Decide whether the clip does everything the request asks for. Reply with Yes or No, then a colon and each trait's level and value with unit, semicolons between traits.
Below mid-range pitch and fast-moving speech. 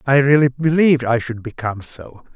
No: low, 130 Hz; average, 180 wpm